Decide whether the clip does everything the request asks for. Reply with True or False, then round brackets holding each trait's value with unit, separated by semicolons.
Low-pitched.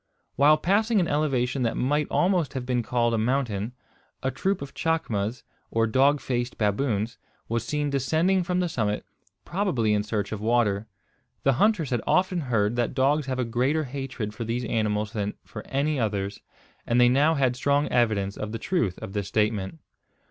True (125 Hz)